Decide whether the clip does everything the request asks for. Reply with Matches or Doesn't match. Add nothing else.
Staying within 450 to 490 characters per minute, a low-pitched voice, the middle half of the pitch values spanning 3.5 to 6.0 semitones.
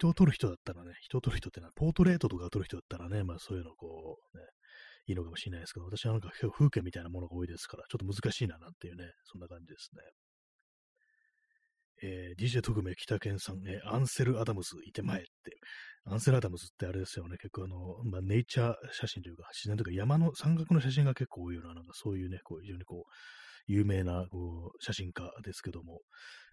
Matches